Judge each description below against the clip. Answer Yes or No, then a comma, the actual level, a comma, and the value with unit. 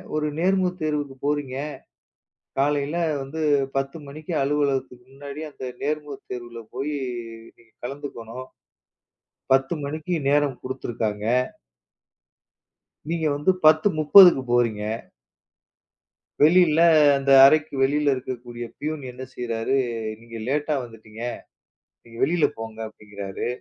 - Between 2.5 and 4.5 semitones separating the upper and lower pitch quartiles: Yes, average, 3.9 semitones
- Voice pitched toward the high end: No, medium, 140 Hz